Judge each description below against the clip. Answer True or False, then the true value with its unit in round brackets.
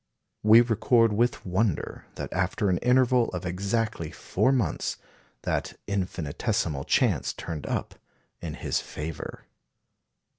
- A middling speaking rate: False (115 wpm)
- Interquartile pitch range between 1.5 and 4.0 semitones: False (5.5 semitones)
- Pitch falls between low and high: False (100 Hz)